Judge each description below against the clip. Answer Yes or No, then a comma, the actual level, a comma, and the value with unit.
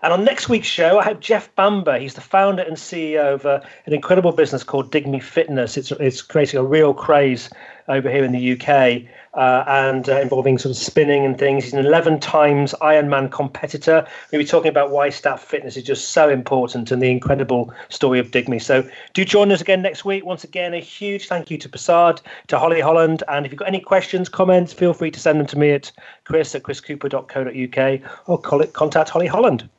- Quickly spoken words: Yes, fast, 215 wpm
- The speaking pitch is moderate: Yes, medium, 150 Hz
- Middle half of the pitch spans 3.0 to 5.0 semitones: Yes, average, 3.9 semitones